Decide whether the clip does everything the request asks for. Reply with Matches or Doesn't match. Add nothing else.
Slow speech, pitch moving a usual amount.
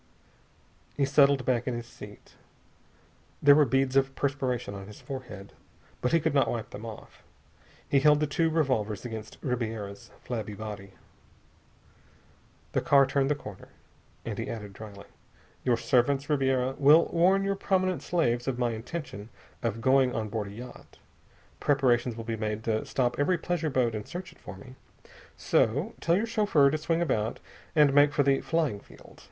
Doesn't match